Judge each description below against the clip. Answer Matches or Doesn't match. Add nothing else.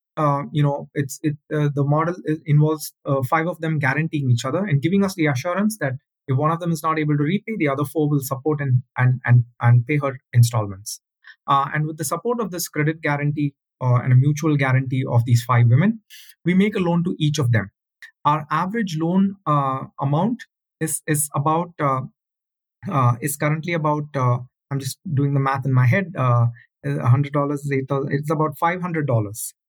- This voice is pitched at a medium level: Matches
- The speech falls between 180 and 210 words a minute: Matches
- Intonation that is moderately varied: Matches